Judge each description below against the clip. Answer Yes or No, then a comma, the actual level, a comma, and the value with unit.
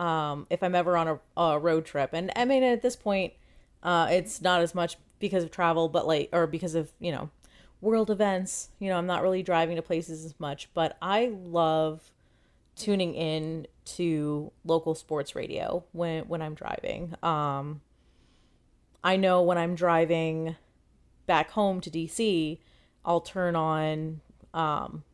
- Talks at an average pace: Yes, average, 165 wpm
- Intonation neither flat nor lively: No, narrow, 2.3 semitones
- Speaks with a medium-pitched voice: Yes, medium, 170 Hz